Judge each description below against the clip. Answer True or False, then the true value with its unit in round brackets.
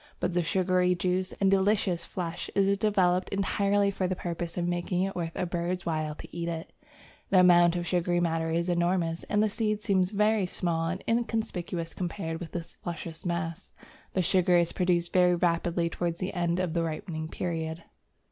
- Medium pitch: True (175 Hz)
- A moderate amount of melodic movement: False (1.9 semitones)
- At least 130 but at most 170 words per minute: False (185 wpm)